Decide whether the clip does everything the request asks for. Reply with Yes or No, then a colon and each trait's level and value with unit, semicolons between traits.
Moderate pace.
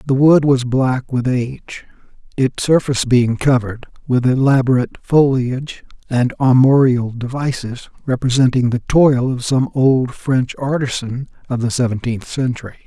No: slow, 130 wpm